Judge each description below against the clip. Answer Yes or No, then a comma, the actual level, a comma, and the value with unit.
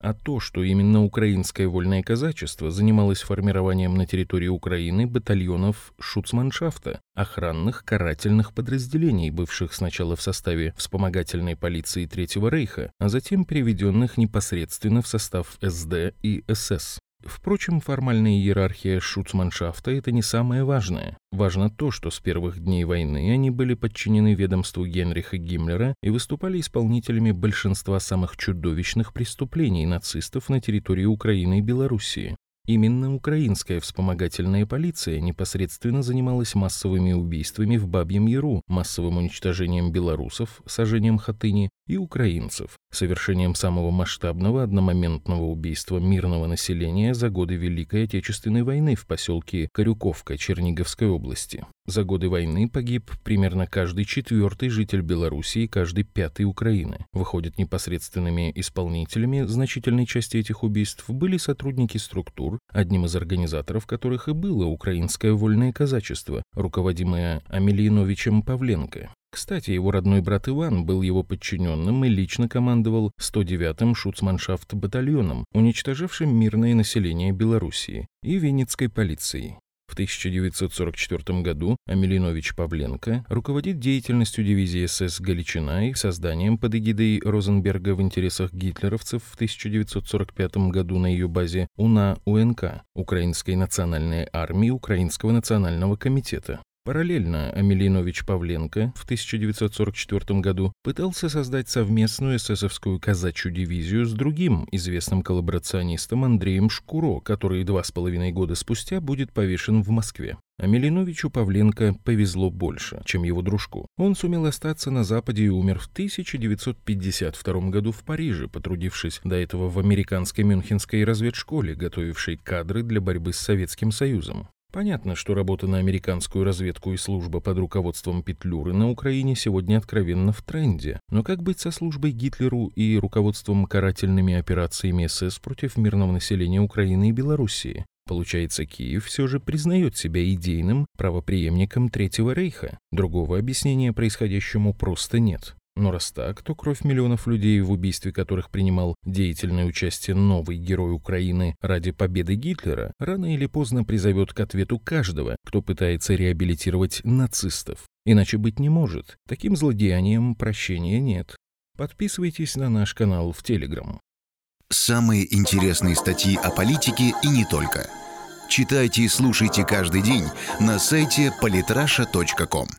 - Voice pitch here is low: Yes, low, 100 Hz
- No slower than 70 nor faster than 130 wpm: Yes, average, 125 wpm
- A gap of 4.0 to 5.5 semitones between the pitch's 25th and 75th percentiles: Yes, average, 4.3 semitones